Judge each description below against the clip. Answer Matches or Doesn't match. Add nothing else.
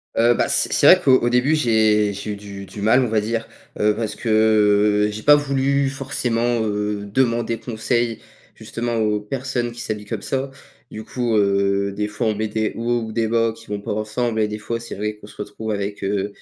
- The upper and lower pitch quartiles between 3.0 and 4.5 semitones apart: Doesn't match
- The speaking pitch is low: Matches